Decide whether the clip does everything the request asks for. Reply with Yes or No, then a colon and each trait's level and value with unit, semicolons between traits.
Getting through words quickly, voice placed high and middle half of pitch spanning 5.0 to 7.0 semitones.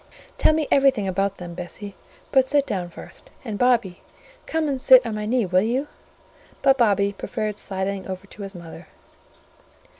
No: average, 170 wpm; high, 210 Hz; average, 5.3 semitones